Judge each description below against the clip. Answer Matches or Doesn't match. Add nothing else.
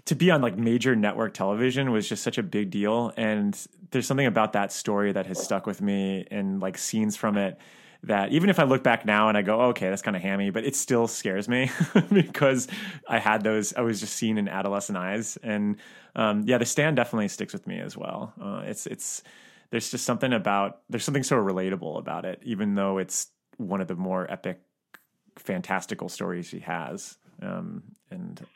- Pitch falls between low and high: Doesn't match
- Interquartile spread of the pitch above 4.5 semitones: Matches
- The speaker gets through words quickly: Matches